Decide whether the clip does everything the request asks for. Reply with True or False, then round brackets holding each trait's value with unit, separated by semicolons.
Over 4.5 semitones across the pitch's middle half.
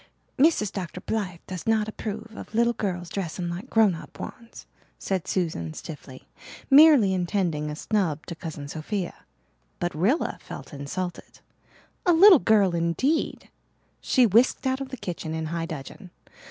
True (5.1 semitones)